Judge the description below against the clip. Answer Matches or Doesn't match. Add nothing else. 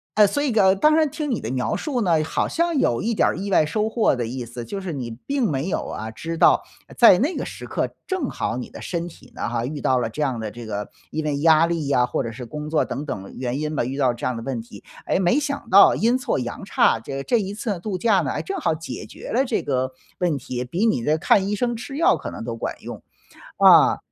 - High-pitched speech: Doesn't match